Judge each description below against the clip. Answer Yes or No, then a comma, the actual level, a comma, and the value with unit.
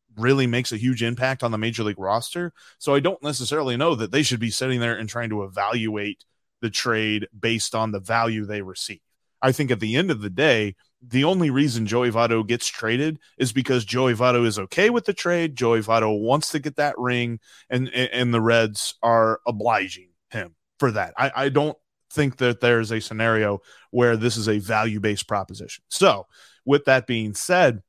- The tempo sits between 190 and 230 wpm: Yes, average, 200 wpm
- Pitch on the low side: Yes, low, 120 Hz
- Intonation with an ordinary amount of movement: Yes, average, 3.3 semitones